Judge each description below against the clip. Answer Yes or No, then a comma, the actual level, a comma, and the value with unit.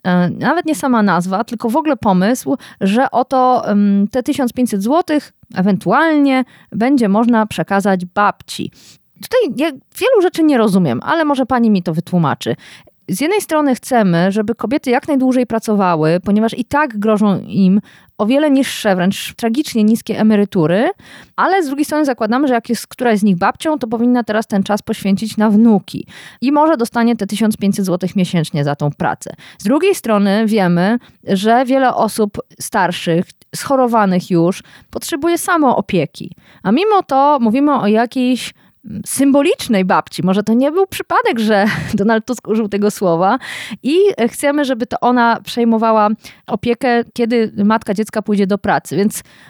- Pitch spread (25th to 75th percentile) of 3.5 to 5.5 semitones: Yes, average, 4.9 semitones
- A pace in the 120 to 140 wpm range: No, average, 155 wpm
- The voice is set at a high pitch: Yes, high, 225 Hz